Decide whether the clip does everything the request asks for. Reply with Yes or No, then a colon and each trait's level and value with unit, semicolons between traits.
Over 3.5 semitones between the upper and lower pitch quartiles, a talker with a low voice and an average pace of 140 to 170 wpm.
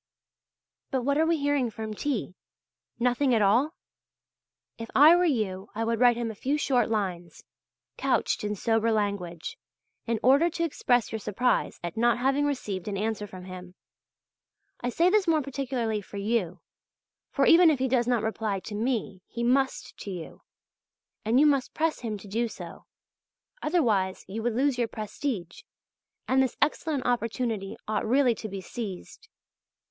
No: average, 4.5 semitones; high, 235 Hz; average, 165 wpm